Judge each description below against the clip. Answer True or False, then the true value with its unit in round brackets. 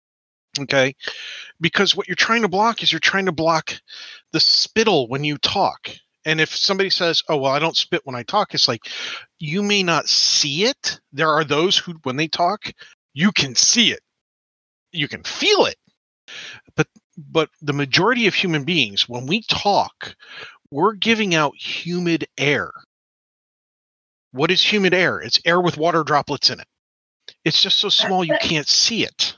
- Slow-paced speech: False (175 wpm)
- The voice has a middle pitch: True (165 Hz)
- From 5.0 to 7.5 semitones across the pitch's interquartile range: True (5.4 semitones)